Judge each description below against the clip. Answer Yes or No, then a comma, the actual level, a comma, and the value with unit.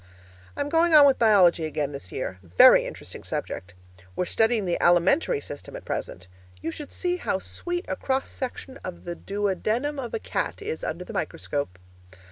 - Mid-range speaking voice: No, high, 205 Hz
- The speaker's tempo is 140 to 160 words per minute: No, average, 175 wpm